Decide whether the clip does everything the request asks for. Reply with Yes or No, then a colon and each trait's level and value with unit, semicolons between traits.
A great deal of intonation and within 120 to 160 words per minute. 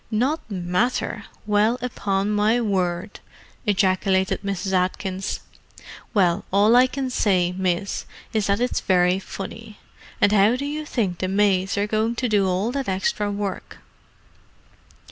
No: average, 3.0 semitones; average, 140 wpm